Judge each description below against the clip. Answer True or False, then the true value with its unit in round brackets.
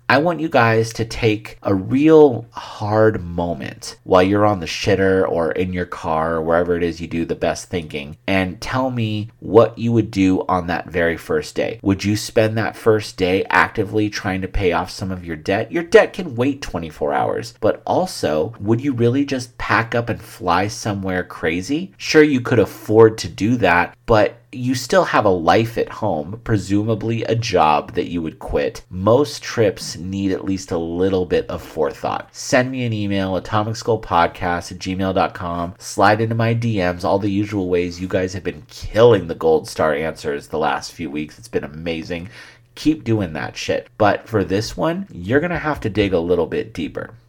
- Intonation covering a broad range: False (3.7 semitones)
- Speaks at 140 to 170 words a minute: False (195 wpm)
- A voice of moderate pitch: False (105 Hz)